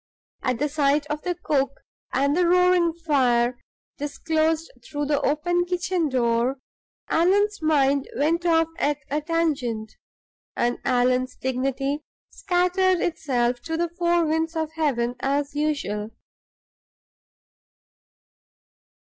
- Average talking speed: No, slow, 115 wpm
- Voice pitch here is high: Yes, very high, 300 Hz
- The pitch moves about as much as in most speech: Yes, average, 4.2 semitones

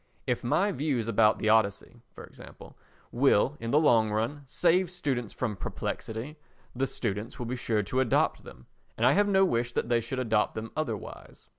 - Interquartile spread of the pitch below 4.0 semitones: No, average, 4.3 semitones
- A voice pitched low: Yes, low, 120 Hz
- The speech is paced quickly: No, average, 185 wpm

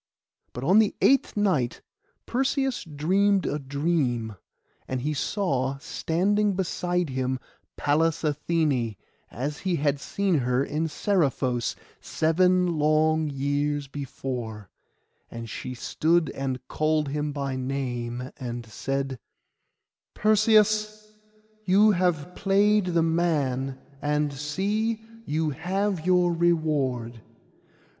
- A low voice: No, medium, 155 Hz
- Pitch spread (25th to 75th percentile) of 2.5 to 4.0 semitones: No, average, 5.3 semitones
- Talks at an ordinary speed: No, slow, 105 wpm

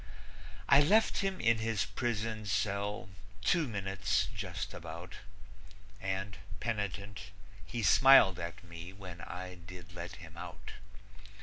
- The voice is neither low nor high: No, low, 100 Hz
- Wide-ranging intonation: No, average, 3.6 semitones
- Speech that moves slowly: Yes, slow, 120 wpm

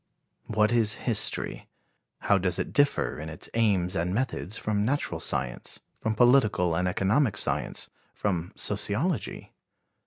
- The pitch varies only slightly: No, average, 4.2 semitones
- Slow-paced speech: Yes, slow, 130 wpm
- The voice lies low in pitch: Yes, low, 105 Hz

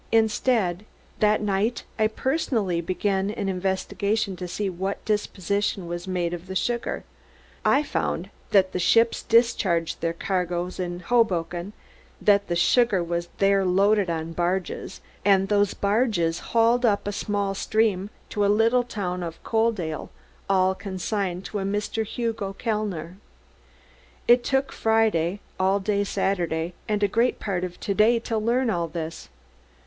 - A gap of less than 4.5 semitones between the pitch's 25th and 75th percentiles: Yes, average, 3.4 semitones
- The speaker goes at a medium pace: Yes, average, 145 wpm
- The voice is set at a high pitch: Yes, high, 195 Hz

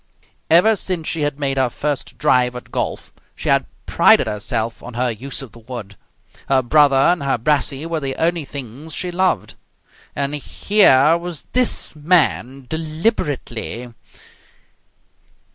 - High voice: No, medium, 140 Hz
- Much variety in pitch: No, average, 4.4 semitones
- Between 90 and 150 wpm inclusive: Yes, average, 145 wpm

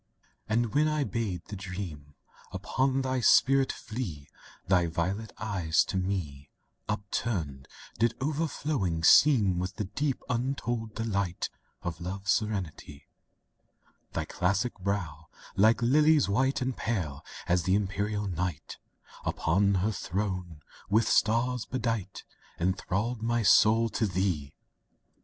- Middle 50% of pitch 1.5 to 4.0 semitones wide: No, average, 4.7 semitones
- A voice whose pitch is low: Yes, low, 100 Hz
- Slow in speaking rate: Yes, slow, 120 wpm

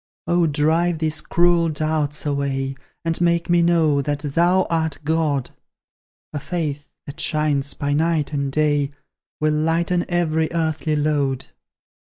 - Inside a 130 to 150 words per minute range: Yes, slow, 135 wpm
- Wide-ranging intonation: No, narrow, 2.5 semitones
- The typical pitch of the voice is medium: Yes, medium, 155 Hz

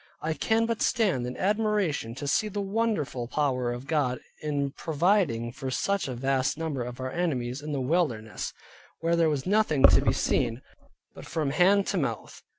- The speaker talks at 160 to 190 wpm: Yes, average, 180 wpm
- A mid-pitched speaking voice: Yes, medium, 150 Hz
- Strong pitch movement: Yes, wide, 6.7 semitones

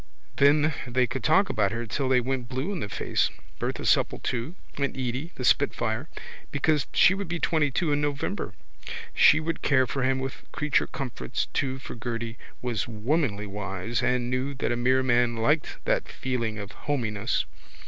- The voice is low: Yes, low, 130 Hz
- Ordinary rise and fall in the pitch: Yes, average, 3.6 semitones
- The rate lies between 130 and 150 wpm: No, average, 175 wpm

